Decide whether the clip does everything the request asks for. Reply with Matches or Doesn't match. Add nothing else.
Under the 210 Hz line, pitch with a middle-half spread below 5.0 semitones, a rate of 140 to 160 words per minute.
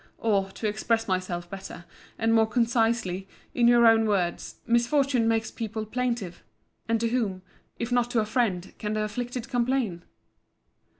Doesn't match